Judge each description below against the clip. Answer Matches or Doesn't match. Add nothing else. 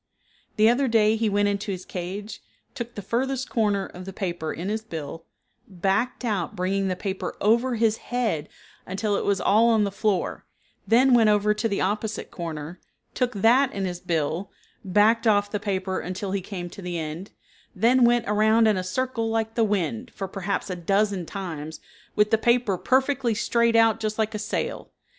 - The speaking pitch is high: Matches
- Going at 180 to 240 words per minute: Matches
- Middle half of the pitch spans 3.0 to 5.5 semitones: Matches